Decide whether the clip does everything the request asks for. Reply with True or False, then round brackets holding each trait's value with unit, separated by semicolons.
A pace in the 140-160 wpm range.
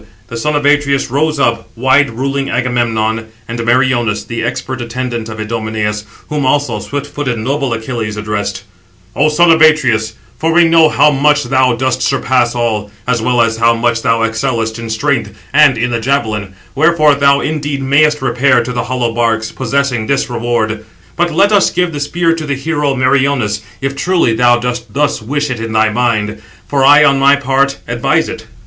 False (185 wpm)